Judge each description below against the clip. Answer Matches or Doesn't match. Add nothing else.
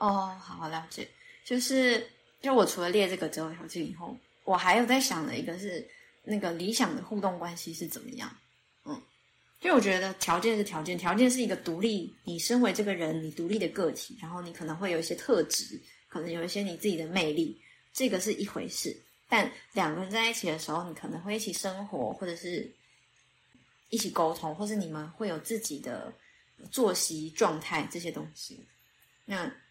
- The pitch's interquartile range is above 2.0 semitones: Matches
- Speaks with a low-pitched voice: Doesn't match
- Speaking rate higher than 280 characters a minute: Matches